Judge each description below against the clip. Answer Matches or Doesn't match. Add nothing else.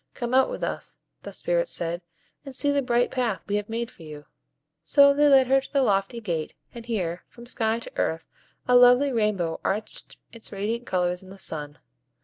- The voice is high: Matches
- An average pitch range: Doesn't match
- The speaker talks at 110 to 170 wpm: Doesn't match